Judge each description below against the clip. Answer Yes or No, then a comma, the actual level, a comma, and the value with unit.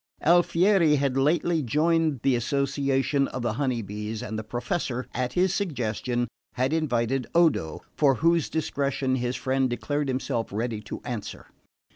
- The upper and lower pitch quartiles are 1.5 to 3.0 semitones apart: No, average, 4.1 semitones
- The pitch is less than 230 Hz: Yes, low, 135 Hz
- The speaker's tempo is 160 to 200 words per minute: No, average, 145 wpm